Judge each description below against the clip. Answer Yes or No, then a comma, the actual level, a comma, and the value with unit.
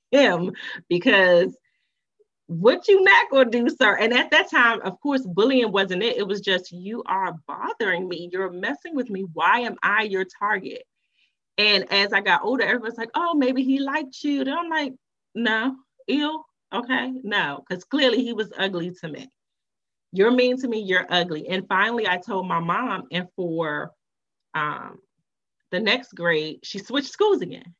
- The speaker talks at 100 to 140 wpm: No, average, 175 wpm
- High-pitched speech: Yes, high, 230 Hz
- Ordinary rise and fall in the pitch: No, wide, 6.6 semitones